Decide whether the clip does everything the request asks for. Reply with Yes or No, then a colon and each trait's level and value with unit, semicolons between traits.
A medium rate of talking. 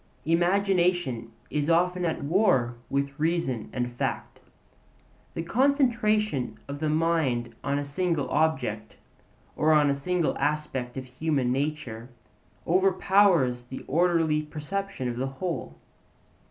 No: slow, 120 wpm